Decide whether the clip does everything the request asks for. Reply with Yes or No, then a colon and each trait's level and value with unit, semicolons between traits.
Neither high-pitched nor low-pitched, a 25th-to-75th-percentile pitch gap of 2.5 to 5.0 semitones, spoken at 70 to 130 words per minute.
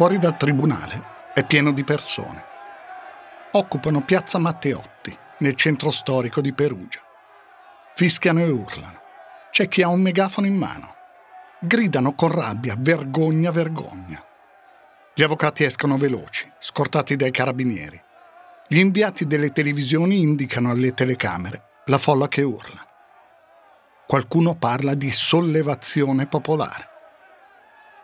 Yes: medium, 150 Hz; average, 4.6 semitones; slow, 115 wpm